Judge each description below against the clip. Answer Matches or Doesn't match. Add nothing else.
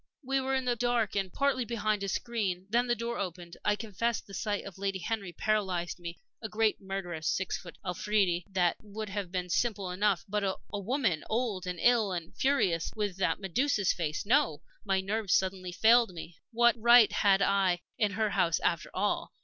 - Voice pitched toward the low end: Doesn't match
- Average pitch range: Matches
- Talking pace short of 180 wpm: Doesn't match